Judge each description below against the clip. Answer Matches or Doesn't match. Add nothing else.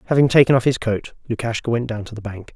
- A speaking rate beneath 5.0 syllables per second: Doesn't match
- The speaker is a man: Matches